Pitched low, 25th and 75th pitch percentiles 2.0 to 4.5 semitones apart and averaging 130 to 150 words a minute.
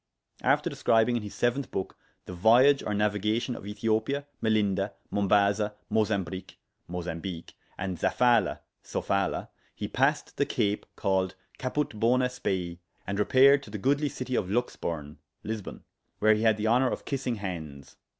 Yes: low, 105 Hz; average, 4.0 semitones; average, 145 wpm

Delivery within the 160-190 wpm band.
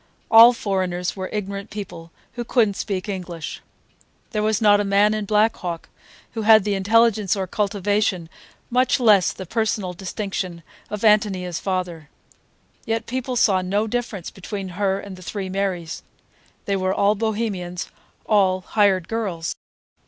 No: average, 150 wpm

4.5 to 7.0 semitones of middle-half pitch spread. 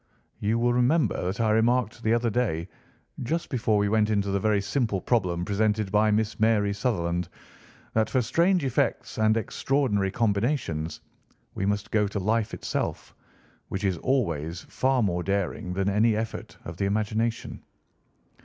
No: average, 2.9 semitones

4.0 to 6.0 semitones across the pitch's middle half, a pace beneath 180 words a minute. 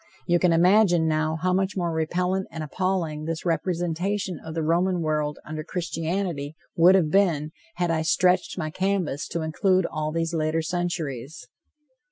No: average, 2.7 semitones; average, 160 wpm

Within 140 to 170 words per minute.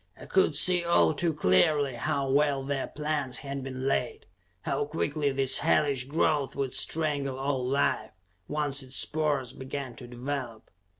Yes: average, 155 wpm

